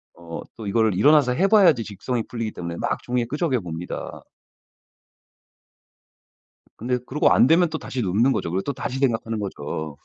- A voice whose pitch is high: No, low, 120 Hz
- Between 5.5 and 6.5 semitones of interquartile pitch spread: Yes, wide, 5.8 semitones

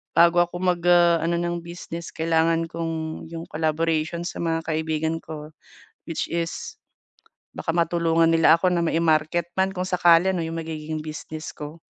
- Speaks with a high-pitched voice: No, medium, 165 Hz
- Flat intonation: Yes, narrow, 1.3 semitones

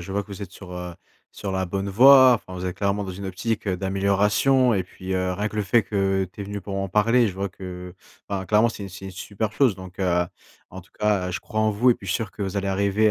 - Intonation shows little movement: Yes, narrow, 2.1 semitones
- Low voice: Yes, low, 100 Hz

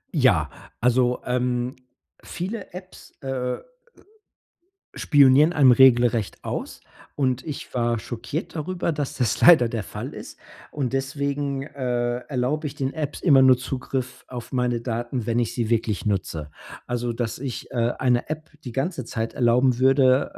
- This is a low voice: Yes, low, 125 Hz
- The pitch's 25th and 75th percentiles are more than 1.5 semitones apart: Yes, narrow, 2.6 semitones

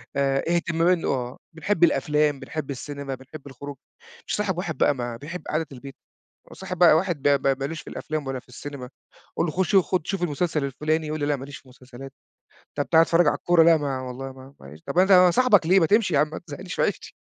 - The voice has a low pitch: No, medium, 150 Hz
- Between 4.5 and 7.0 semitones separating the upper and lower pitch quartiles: No, average, 4.0 semitones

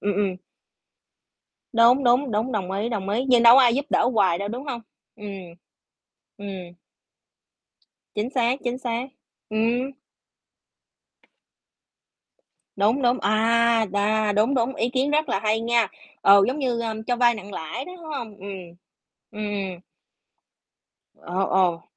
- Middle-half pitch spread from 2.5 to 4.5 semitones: Yes, average, 3.4 semitones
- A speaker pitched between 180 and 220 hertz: No, high, 230 Hz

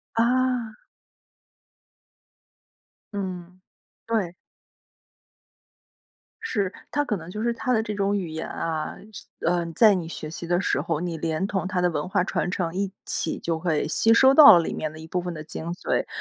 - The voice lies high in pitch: No, medium, 180 Hz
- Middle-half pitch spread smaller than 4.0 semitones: No, average, 4.3 semitones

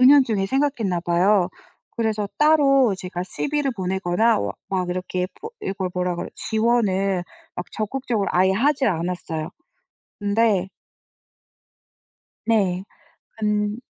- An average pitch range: Yes, average, 4.3 semitones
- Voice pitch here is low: No, high, 200 Hz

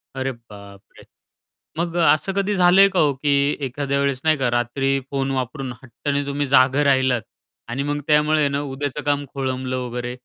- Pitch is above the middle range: No, low, 135 Hz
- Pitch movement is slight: Yes, narrow, 2.2 semitones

